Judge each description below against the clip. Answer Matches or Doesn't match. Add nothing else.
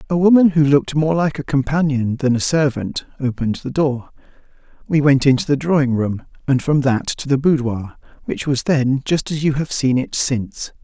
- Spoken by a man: Matches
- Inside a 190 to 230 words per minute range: Matches